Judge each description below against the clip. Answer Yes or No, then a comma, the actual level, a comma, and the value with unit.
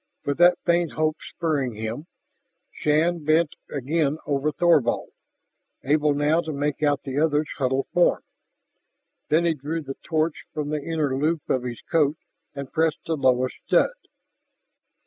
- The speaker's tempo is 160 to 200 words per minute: No, average, 145 wpm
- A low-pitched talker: No, medium, 150 Hz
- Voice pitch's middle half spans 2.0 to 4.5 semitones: Yes, narrow, 2.6 semitones